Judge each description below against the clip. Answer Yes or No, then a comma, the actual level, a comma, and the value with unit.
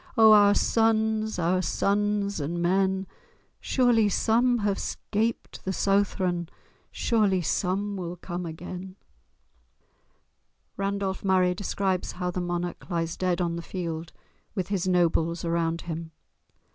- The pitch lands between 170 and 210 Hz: Yes, medium, 185 Hz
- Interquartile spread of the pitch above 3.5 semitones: No, average, 2.8 semitones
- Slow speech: Yes, slow, 120 wpm